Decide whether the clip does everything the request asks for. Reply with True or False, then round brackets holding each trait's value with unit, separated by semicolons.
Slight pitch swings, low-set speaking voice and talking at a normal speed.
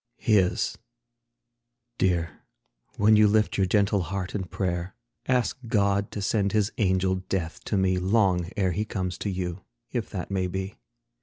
True (2.1 semitones; 95 Hz; 155 wpm)